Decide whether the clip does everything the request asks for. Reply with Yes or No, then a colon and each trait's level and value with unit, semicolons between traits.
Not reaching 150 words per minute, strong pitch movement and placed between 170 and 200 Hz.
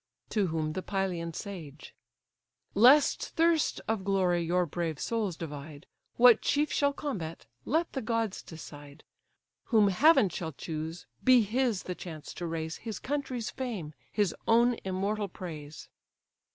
Yes: average, 140 wpm; wide, 6.2 semitones; high, 190 Hz